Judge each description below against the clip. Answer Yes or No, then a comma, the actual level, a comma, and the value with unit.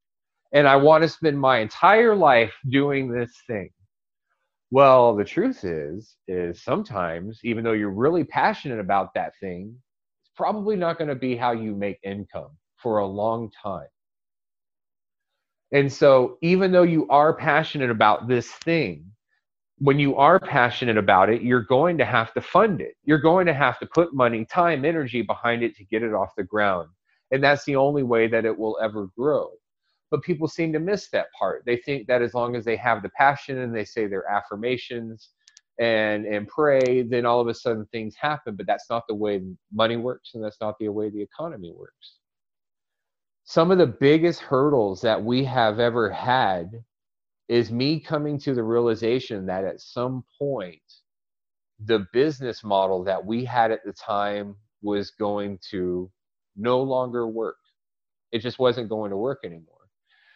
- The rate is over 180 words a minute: No, average, 175 wpm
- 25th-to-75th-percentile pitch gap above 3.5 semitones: Yes, average, 4.8 semitones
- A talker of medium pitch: No, low, 120 Hz